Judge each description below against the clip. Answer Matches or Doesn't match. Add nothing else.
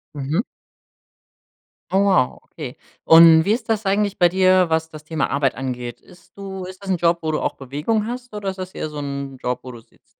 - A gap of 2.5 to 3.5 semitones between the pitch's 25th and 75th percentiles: Doesn't match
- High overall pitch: Doesn't match